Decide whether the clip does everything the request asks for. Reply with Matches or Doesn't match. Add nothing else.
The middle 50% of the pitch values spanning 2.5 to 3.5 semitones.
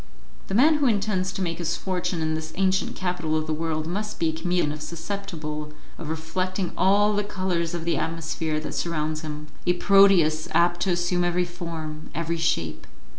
Matches